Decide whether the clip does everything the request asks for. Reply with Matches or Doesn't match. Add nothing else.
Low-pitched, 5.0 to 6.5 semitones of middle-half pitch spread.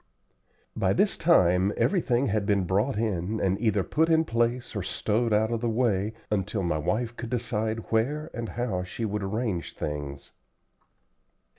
Doesn't match